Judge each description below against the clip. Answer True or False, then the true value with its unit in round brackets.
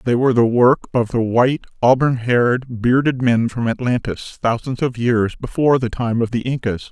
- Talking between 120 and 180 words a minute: False (190 wpm)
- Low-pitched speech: True (120 Hz)